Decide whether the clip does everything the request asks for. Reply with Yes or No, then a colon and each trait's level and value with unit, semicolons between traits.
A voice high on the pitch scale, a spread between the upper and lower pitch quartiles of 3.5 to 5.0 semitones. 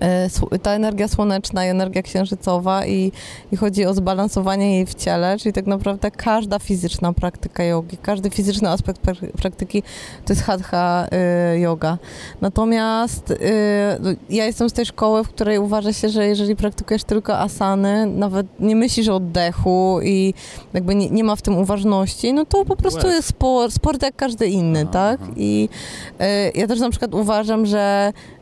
No: high, 200 Hz; narrow, 2.4 semitones